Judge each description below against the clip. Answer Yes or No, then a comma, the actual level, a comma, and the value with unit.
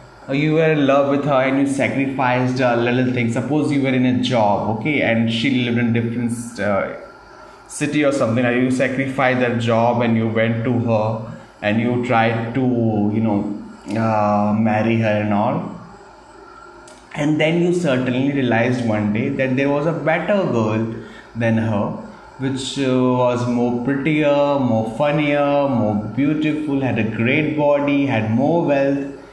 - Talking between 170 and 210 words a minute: No, average, 160 wpm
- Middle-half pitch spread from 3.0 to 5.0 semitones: Yes, average, 3.5 semitones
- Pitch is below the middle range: Yes, low, 125 Hz